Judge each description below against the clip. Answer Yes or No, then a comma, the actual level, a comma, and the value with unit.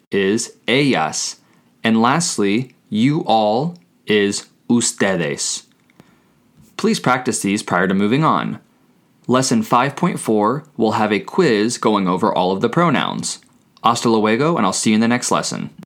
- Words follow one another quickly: No, average, 140 wpm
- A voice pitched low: Yes, low, 115 Hz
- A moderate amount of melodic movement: Yes, average, 4.0 semitones